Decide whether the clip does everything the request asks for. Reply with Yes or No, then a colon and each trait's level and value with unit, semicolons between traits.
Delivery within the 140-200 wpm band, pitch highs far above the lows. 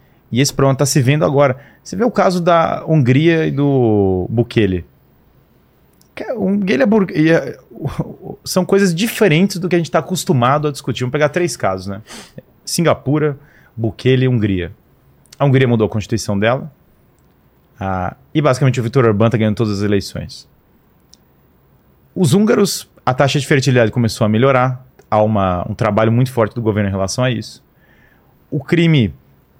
Yes: average, 165 wpm; wide, 6.2 semitones